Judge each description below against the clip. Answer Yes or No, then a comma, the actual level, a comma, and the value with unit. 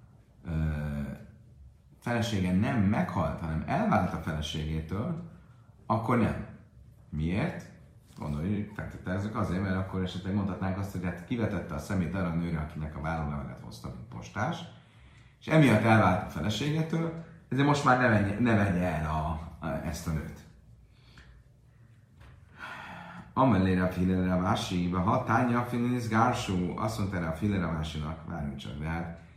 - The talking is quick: No, average, 130 wpm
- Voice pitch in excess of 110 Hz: No, very low, 95 Hz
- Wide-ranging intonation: Yes, wide, 5.8 semitones